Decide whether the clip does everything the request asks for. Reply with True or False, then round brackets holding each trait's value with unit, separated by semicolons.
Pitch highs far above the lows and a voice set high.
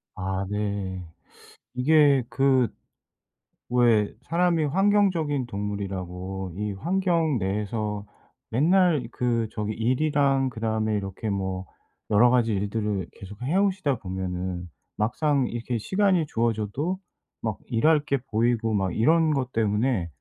False (6.2 semitones; 115 Hz)